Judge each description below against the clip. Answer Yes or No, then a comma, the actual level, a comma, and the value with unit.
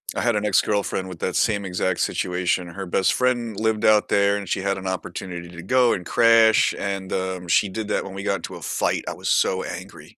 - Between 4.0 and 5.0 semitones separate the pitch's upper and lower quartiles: No, narrow, 2.5 semitones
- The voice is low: Yes, low, 100 Hz